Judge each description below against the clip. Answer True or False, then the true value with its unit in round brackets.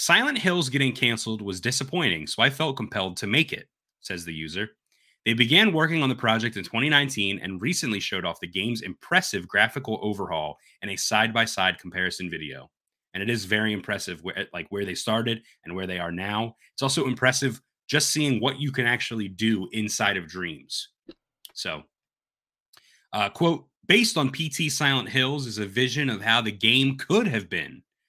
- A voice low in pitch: True (115 Hz)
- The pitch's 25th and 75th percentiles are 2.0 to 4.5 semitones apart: False (5.5 semitones)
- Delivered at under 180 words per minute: False (185 wpm)